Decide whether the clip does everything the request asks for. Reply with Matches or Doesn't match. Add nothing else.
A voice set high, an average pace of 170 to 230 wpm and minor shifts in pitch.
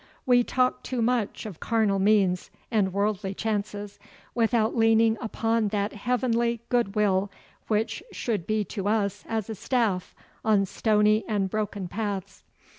Doesn't match